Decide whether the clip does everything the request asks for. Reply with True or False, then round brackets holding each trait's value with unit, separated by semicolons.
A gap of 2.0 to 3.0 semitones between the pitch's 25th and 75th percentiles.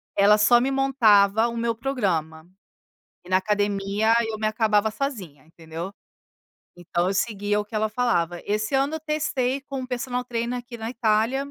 False (3.8 semitones)